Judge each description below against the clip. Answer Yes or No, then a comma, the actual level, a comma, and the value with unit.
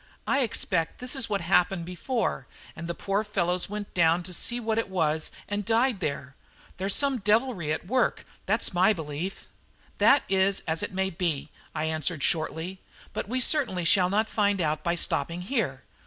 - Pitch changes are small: No, average, 4.5 semitones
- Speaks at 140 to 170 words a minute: No, average, 180 wpm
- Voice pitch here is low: No, medium, 185 Hz